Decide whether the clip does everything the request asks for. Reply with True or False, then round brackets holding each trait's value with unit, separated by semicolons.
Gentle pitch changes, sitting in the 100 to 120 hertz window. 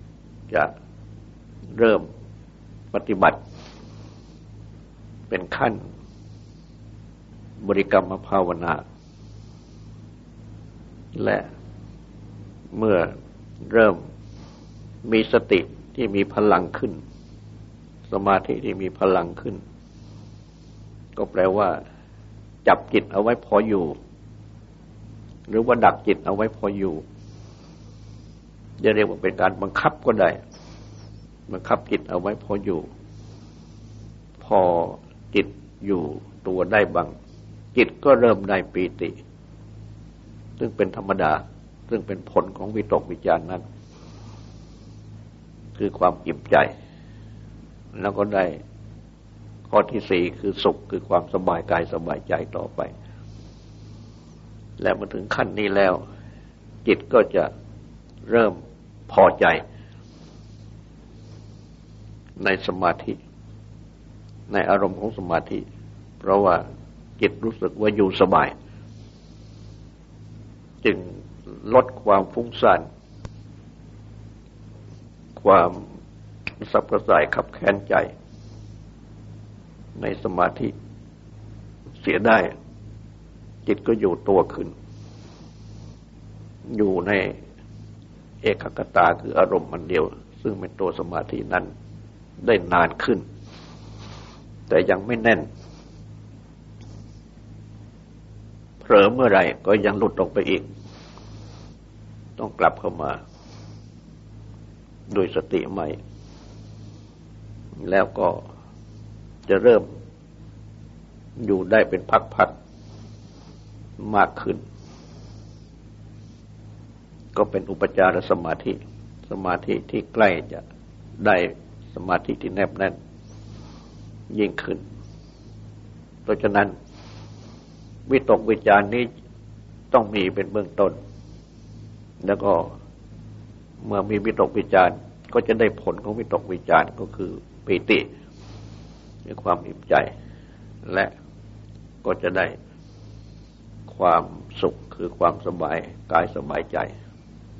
True (1.9 semitones; 105 Hz)